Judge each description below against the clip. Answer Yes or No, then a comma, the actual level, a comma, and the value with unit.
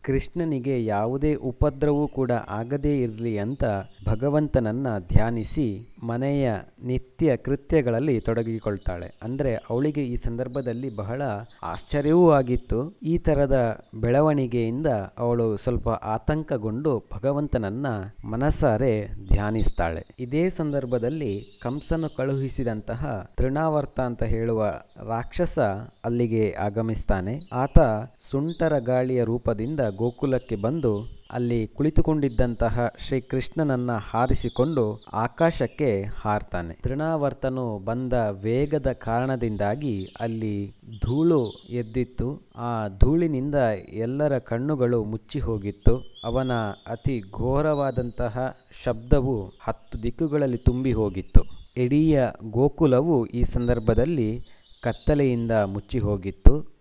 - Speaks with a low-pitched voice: Yes, low, 120 Hz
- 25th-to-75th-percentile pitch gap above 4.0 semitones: No, average, 3.7 semitones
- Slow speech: No, average, 85 wpm